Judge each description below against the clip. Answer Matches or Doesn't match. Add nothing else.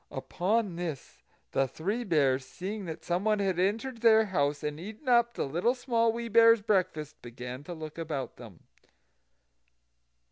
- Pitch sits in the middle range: Matches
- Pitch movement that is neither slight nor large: Doesn't match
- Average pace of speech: Matches